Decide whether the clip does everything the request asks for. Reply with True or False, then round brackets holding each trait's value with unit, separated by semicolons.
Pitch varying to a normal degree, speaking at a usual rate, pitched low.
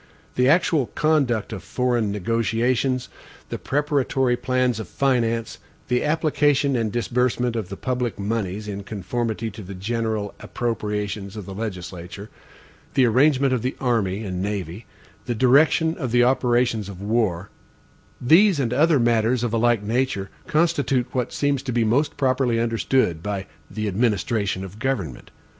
True (3.8 semitones; 150 wpm; 120 Hz)